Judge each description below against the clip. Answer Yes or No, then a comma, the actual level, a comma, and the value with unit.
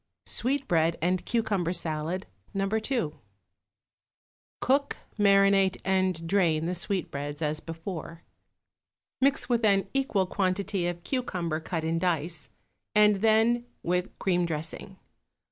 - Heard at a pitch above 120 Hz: Yes, medium, 185 Hz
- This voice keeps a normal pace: No, slow, 110 wpm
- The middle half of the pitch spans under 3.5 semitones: No, average, 4.0 semitones